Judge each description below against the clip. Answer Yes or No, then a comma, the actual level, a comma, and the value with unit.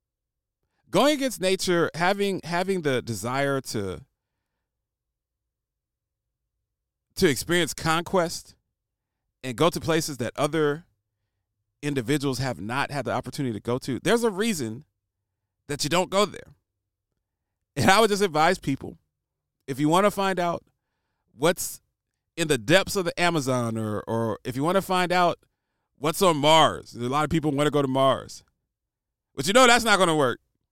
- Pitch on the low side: No, medium, 145 Hz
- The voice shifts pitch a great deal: Yes, wide, 7.5 semitones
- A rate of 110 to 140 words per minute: No, average, 160 wpm